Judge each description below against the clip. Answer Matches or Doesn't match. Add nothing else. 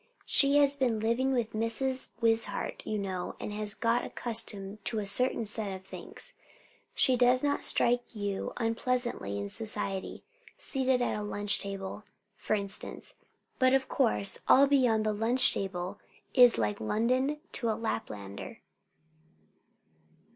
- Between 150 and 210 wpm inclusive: Doesn't match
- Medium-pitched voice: Doesn't match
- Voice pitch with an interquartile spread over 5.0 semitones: Doesn't match